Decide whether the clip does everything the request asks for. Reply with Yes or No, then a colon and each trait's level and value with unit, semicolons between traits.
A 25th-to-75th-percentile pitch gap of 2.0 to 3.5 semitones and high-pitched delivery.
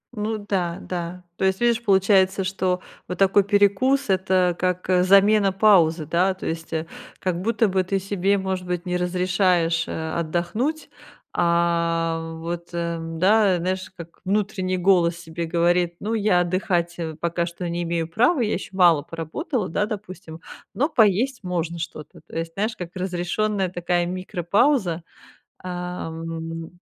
No: narrow, 2.6 semitones; medium, 180 Hz